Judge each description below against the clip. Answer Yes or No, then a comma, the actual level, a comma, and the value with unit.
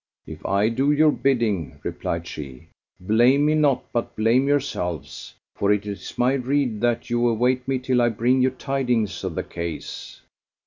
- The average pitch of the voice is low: Yes, low, 120 Hz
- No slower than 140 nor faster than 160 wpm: No, average, 170 wpm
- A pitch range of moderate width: Yes, average, 4.3 semitones